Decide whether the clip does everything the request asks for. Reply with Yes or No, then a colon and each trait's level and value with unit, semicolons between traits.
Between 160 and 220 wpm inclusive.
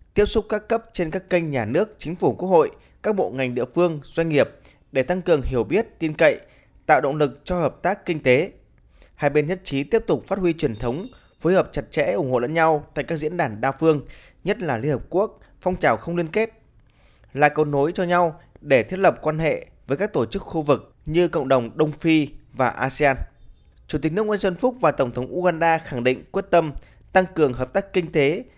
No: average, 235 wpm